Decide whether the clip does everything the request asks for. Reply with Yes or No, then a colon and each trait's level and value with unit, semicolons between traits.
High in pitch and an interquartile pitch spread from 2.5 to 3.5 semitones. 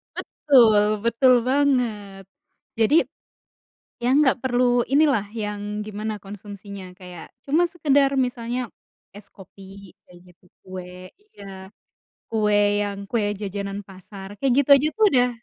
No: high, 210 Hz; average, 4.1 semitones